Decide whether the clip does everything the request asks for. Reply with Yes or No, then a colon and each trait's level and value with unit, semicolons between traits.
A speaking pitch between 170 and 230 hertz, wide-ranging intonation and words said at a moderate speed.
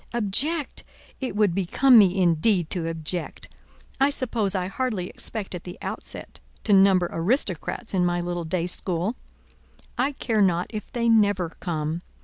No: high, 190 Hz; average, 4.4 semitones; average, 150 wpm